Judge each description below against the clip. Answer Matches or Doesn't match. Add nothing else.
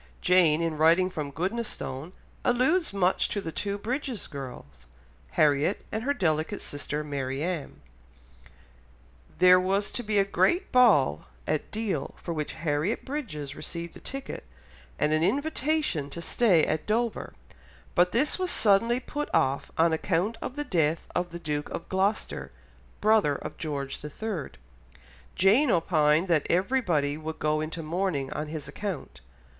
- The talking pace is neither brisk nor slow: Matches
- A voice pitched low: Doesn't match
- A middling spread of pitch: Doesn't match